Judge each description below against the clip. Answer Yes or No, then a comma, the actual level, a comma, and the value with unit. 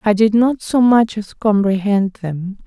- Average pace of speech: Yes, average, 180 wpm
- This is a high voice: Yes, high, 210 Hz